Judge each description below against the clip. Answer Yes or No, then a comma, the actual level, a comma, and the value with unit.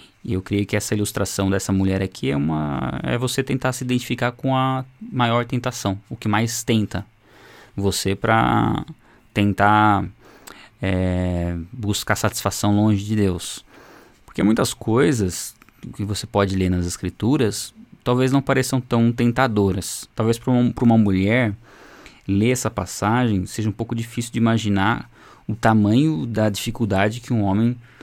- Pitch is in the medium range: No, low, 110 Hz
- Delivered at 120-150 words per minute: Yes, average, 145 wpm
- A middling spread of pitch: Yes, average, 3.5 semitones